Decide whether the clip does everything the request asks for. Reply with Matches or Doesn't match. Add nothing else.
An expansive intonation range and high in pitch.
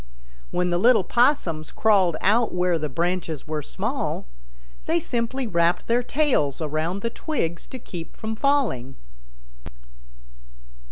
Doesn't match